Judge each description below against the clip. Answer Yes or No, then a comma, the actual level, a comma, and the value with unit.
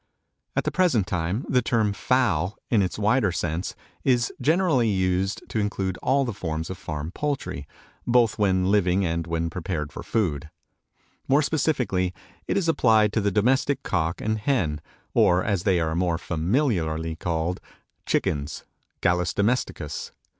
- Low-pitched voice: Yes, very low, 95 Hz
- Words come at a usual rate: Yes, average, 150 wpm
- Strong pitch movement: Yes, wide, 6.0 semitones